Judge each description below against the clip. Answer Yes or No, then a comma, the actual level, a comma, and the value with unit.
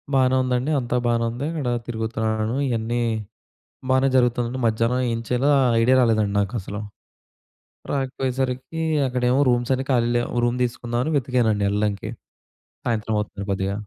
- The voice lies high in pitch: No, low, 120 Hz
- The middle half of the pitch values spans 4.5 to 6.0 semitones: No, narrow, 2.4 semitones